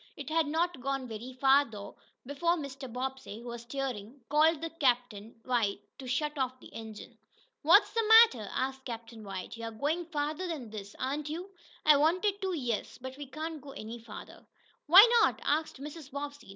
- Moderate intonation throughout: Yes, average, 4.7 semitones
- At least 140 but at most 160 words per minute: No, average, 180 wpm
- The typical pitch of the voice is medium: No, very high, 270 Hz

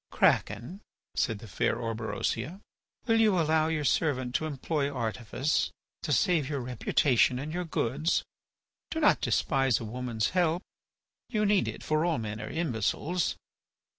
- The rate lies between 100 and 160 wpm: Yes, average, 145 wpm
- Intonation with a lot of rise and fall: Yes, wide, 5.8 semitones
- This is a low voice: No, medium, 145 Hz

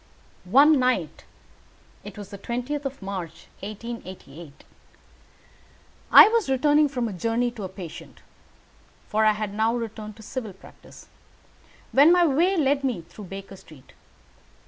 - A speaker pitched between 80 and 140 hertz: No, high, 225 Hz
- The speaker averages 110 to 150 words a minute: Yes, average, 145 wpm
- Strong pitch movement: Yes, wide, 5.7 semitones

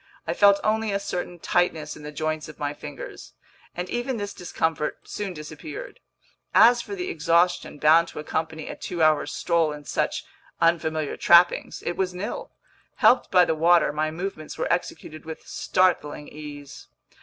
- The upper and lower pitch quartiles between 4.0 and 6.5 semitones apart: No, average, 3.3 semitones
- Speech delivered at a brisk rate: No, average, 160 wpm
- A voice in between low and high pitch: Yes, medium, 170 Hz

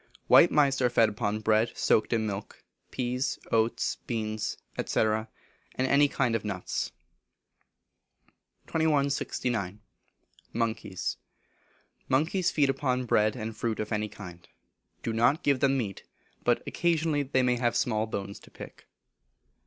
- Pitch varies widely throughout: No, average, 4.0 semitones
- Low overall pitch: Yes, low, 115 Hz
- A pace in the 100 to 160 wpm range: Yes, slow, 135 wpm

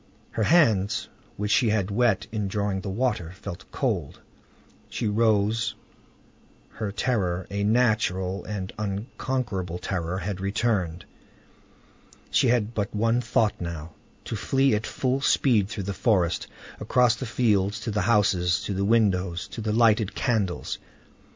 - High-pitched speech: No, low, 105 Hz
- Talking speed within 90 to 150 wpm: Yes, average, 140 wpm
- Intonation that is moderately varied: Yes, average, 3.3 semitones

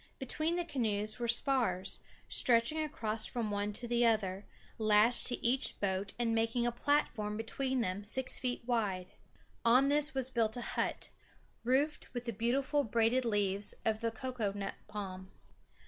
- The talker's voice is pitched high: Yes, high, 230 Hz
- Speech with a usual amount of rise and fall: Yes, average, 3.5 semitones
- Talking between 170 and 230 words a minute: No, average, 160 wpm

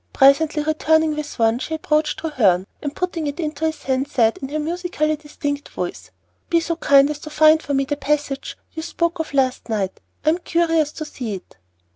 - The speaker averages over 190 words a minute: Yes, average, 200 wpm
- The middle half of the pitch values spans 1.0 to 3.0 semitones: Yes, narrow, 2.6 semitones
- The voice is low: No, very high, 300 Hz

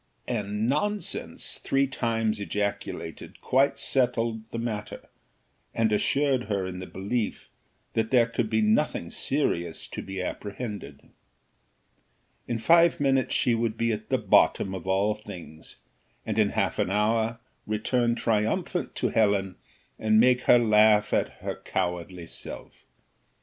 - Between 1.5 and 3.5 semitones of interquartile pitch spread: Yes, average, 2.8 semitones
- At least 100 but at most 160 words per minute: Yes, slow, 135 wpm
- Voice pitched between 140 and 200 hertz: No, low, 110 Hz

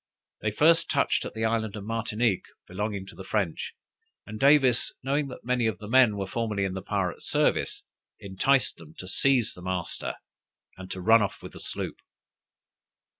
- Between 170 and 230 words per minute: Yes, average, 175 wpm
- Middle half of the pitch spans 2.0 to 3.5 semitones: No, average, 4.4 semitones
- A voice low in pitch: Yes, low, 105 Hz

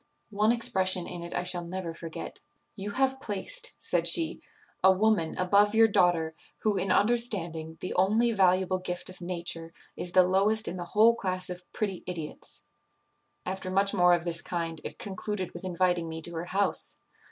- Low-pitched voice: No, medium, 185 Hz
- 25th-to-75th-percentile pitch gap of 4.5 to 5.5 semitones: No, average, 2.9 semitones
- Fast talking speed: No, average, 175 wpm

